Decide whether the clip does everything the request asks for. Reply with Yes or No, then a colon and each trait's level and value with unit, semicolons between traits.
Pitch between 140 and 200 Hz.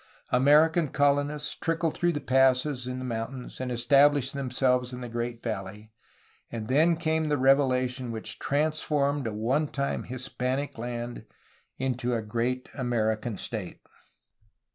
No: low, 130 Hz